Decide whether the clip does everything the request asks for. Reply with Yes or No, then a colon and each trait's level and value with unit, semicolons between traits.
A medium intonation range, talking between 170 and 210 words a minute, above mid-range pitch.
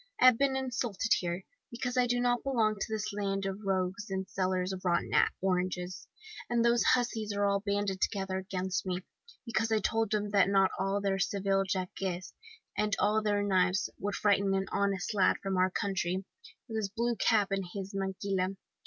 No: narrow, 2.3 semitones; average, 180 wpm; high, 200 Hz